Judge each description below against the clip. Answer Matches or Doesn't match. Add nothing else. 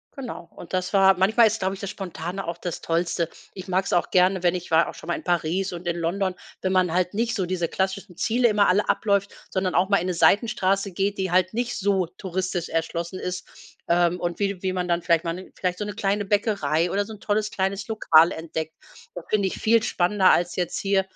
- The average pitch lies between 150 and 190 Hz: Matches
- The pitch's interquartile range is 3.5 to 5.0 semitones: Doesn't match